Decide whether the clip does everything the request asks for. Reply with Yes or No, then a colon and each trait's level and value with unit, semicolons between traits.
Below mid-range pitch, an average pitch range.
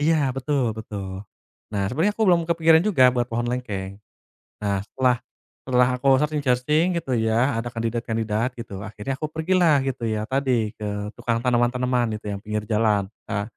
Yes: low, 120 Hz; average, 4.2 semitones